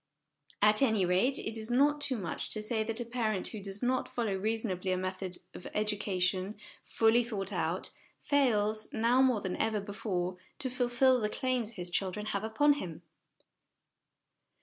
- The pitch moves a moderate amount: Yes, average, 4.0 semitones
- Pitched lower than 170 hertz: No, high, 215 Hz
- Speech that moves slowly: No, average, 170 wpm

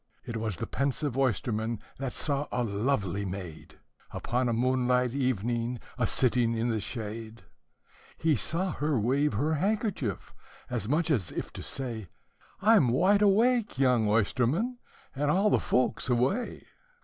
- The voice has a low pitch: Yes, low, 125 Hz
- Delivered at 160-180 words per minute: No, average, 150 wpm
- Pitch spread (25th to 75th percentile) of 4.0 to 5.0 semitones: Yes, average, 4.7 semitones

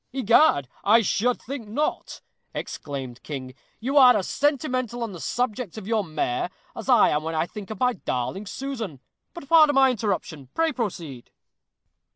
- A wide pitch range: Yes, wide, 7.9 semitones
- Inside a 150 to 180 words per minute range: Yes, average, 165 wpm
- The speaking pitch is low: No, high, 220 Hz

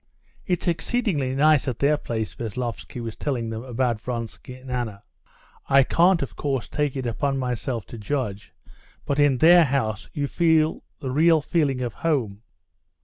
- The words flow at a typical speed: Yes, average, 160 wpm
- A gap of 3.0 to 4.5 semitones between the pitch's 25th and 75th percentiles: Yes, average, 4.0 semitones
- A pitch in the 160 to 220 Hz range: No, low, 130 Hz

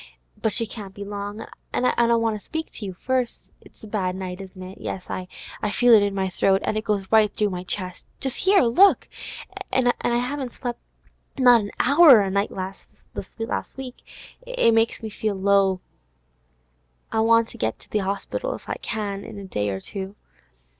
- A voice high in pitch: Yes, high, 215 Hz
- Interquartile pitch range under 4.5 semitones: Yes, average, 3.6 semitones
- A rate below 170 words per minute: No, average, 195 wpm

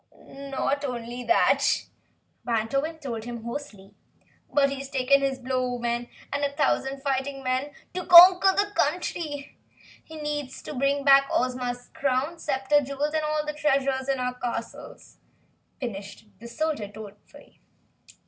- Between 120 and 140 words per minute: Yes, slow, 135 wpm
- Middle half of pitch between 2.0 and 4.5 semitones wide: Yes, average, 2.9 semitones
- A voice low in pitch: No, very high, 275 Hz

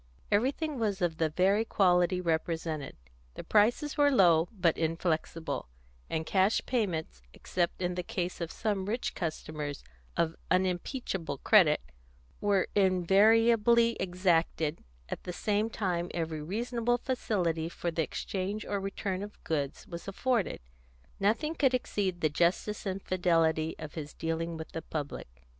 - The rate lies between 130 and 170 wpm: Yes, average, 140 wpm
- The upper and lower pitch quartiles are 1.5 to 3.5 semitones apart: No, average, 4.2 semitones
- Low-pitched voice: No, medium, 185 Hz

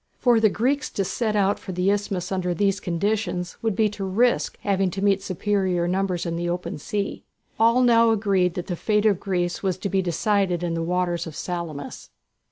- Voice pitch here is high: Yes, high, 195 Hz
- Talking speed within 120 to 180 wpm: No, average, 200 wpm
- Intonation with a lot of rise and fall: No, average, 2.8 semitones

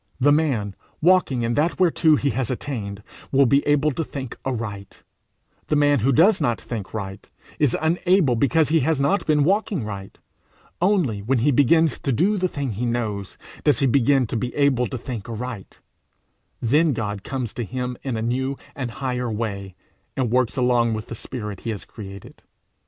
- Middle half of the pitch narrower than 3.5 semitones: No, average, 4.4 semitones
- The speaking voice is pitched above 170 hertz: No, low, 130 Hz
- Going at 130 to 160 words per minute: No, average, 185 wpm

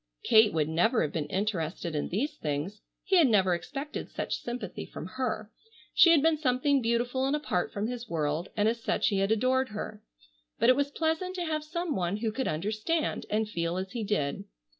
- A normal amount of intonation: No, wide, 6.7 semitones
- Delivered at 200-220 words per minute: Yes, fast, 205 wpm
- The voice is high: Yes, high, 220 Hz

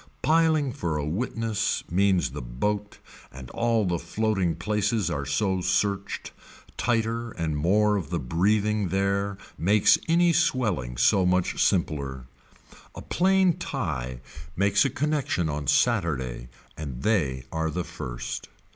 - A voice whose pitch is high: No, very low, 95 Hz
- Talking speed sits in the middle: No, slow, 130 wpm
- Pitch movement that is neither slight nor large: No, wide, 6.5 semitones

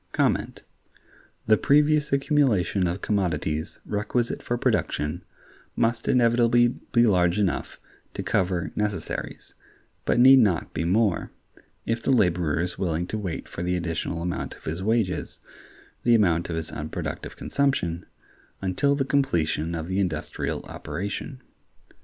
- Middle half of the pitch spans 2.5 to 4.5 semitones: No, wide, 5.6 semitones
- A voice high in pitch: No, low, 100 Hz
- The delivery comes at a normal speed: No, slow, 130 wpm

